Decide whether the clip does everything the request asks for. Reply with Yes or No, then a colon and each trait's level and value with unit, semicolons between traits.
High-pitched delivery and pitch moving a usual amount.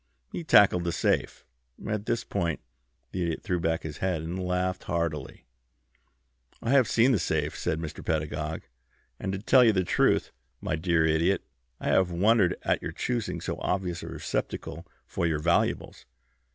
No: very low, 90 Hz; average, 3.2 semitones